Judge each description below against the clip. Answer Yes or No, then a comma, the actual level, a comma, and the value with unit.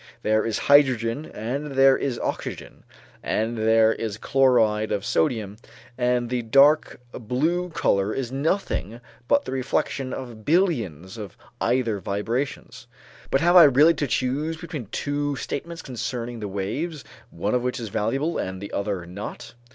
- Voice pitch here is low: Yes, low, 125 Hz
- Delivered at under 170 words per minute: Yes, average, 150 wpm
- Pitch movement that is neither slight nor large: Yes, average, 4.7 semitones